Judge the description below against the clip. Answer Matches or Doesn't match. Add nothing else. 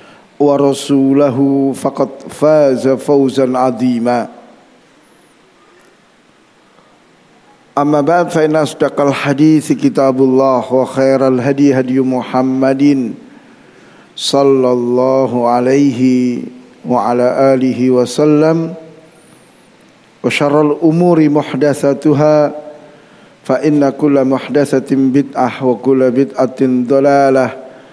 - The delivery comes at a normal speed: Doesn't match